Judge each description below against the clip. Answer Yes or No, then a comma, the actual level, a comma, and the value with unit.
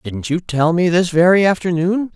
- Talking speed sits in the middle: Yes, average, 195 wpm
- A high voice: No, medium, 175 Hz